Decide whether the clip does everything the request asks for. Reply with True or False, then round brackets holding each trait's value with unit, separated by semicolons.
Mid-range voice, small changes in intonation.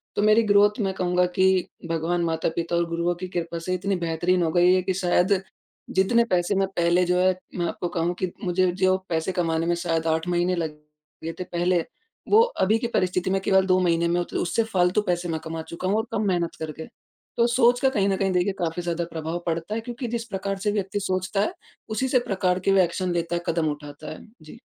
True (180 Hz; 2.3 semitones)